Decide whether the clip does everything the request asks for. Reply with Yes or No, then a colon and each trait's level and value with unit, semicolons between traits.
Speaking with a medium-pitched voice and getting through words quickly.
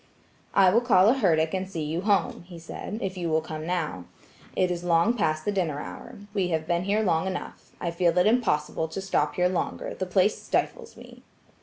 Yes: medium, 180 Hz; fast, 210 wpm